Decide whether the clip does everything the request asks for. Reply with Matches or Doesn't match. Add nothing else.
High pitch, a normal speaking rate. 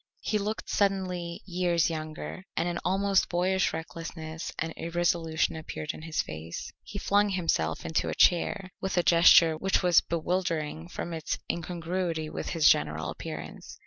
Doesn't match